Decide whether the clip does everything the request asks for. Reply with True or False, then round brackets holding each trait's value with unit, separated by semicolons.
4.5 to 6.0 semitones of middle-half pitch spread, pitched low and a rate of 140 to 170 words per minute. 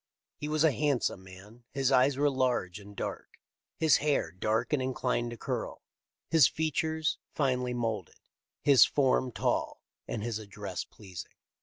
True (5.2 semitones; 125 Hz; 150 wpm)